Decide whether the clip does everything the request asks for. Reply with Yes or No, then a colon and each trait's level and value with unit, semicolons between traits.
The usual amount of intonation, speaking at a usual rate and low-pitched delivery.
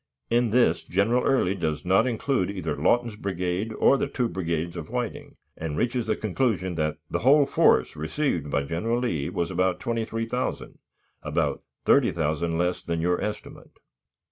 No: wide, 6.0 semitones; average, 155 wpm; very low, 95 Hz